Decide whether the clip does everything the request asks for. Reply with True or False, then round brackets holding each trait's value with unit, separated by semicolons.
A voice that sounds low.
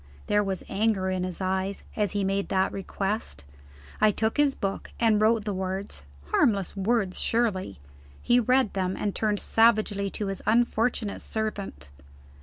False (205 Hz)